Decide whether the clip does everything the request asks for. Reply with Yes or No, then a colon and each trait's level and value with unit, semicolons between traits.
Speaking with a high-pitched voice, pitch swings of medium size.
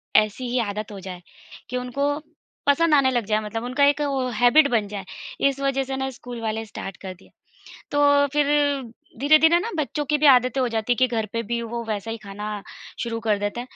Yes: high, 245 Hz; average, 4.4 semitones